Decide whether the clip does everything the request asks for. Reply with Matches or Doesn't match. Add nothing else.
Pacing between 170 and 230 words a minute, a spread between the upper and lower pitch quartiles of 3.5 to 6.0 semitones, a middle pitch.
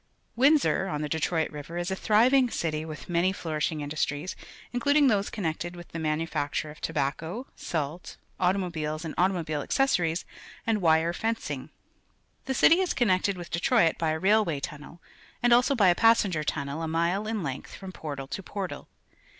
Matches